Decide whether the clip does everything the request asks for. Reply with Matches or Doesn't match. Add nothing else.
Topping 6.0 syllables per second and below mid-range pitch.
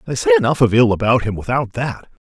Matches